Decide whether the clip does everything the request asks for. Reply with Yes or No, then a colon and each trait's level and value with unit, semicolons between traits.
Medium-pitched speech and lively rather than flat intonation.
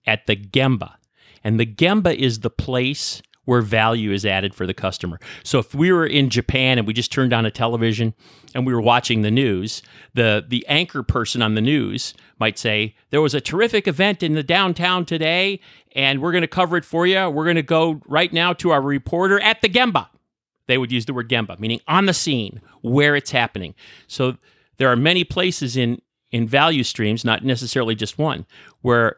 No: low, 130 Hz; wide, 6.1 semitones